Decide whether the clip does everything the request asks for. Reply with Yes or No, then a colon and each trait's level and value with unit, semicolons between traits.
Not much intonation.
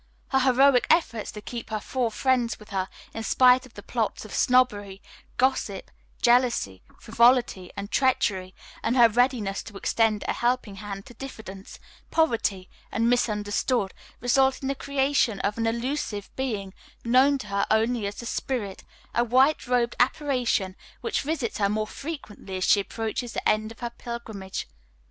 No: average, 3.8 semitones